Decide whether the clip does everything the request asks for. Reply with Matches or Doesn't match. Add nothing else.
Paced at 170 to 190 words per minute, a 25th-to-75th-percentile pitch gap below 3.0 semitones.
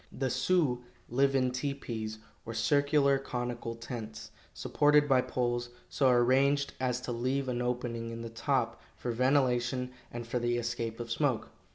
Doesn't match